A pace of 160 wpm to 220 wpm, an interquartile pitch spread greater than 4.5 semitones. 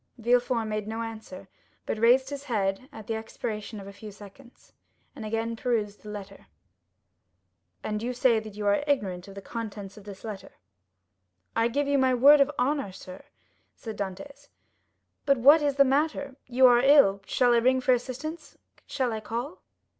No: average, 170 wpm; average, 3.9 semitones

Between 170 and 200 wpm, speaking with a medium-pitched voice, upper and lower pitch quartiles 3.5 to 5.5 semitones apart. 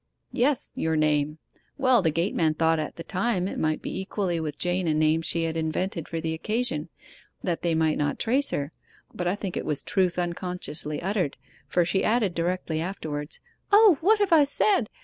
Yes: average, 190 wpm; medium, 175 Hz; average, 4.3 semitones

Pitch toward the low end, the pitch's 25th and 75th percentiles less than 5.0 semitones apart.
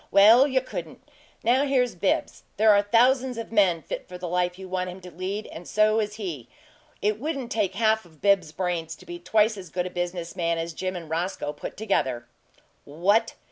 No: high, 190 Hz; average, 3.9 semitones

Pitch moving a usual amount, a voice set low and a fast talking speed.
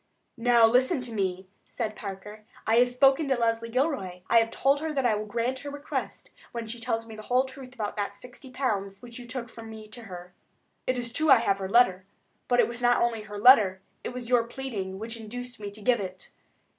No: average, 3.0 semitones; high, 230 Hz; fast, 230 wpm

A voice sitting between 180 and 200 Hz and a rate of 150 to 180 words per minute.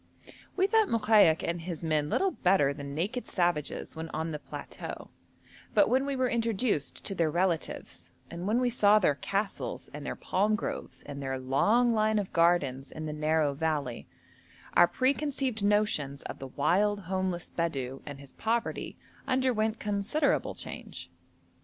Yes: medium, 185 Hz; average, 160 wpm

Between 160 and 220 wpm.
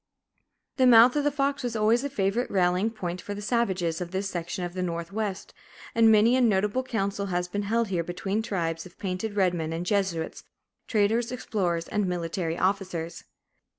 Yes: average, 185 wpm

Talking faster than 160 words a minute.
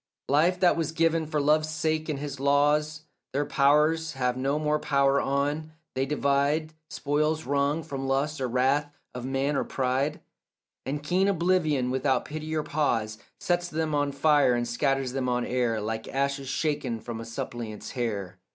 Yes: average, 170 wpm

